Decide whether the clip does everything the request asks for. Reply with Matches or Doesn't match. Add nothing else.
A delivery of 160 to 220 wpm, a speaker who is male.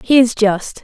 Doesn't match